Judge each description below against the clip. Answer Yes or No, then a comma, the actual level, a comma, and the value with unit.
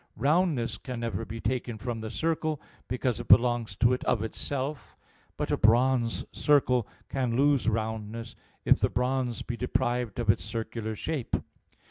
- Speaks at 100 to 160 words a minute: Yes, average, 155 wpm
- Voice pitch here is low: Yes, low, 120 Hz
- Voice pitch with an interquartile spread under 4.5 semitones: Yes, narrow, 2.5 semitones